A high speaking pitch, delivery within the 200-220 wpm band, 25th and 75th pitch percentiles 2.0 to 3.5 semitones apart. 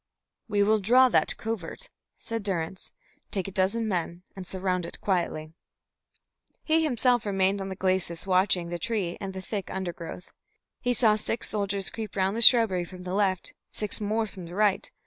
No: high, 195 Hz; average, 175 wpm; average, 3.0 semitones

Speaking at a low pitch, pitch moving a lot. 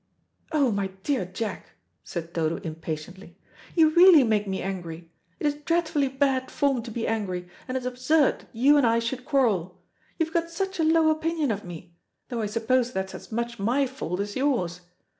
No: high, 240 Hz; wide, 7.1 semitones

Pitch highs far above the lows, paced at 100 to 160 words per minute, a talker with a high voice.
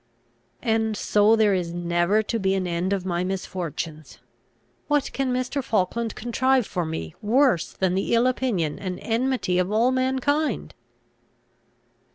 Yes: wide, 5.7 semitones; average, 150 wpm; high, 210 Hz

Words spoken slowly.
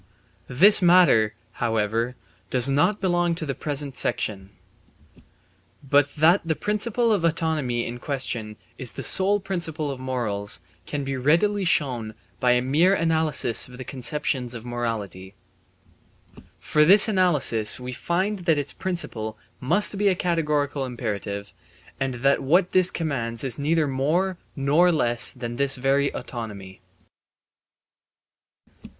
Yes: slow, 130 wpm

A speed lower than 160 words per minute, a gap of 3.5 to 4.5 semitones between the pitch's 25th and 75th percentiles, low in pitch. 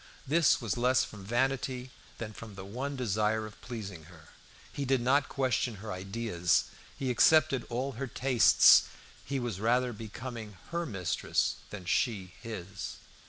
Yes: average, 150 wpm; average, 4.2 semitones; low, 115 Hz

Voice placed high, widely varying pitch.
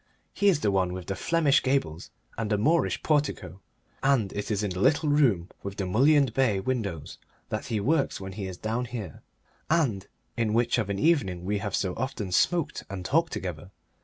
No: low, 110 Hz; wide, 6.3 semitones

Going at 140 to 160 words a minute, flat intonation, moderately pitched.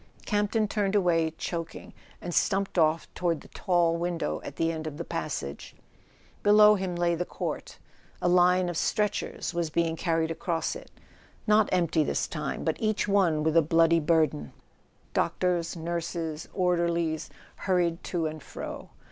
Yes: average, 155 wpm; narrow, 2.0 semitones; medium, 170 Hz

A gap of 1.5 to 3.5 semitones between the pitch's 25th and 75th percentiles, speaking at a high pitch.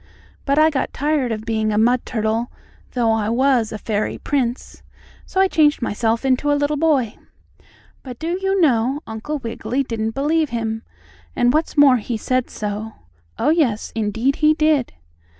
No: average, 4.8 semitones; very high, 250 Hz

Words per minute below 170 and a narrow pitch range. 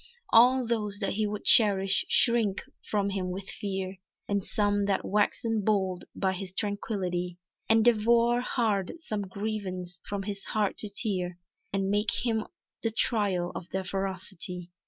Yes: average, 150 wpm; narrow, 2.3 semitones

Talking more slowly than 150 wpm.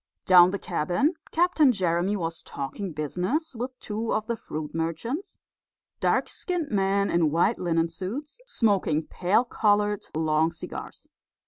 Yes: average, 140 wpm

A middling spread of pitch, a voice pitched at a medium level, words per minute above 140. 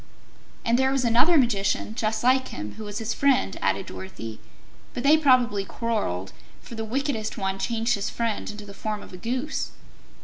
No: average, 4.1 semitones; high, 225 Hz; average, 180 wpm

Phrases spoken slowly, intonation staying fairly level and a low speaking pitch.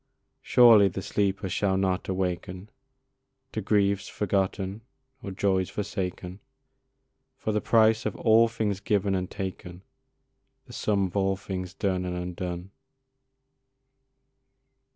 Yes: slow, 115 wpm; narrow, 2.0 semitones; very low, 95 Hz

